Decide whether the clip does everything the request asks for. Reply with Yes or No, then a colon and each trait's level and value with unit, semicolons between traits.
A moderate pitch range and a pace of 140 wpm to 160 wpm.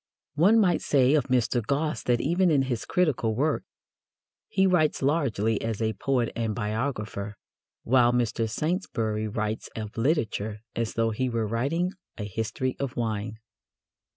Yes: average, 4.7 semitones; average, 150 wpm